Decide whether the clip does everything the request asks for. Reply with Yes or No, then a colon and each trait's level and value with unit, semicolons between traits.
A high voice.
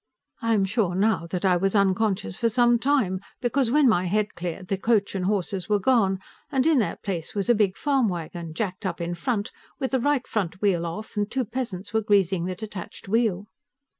Yes: high, 205 Hz